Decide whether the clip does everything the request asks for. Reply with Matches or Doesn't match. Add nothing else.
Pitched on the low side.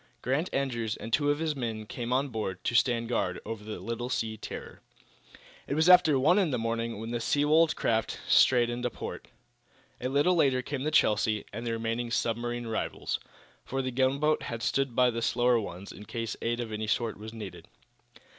Matches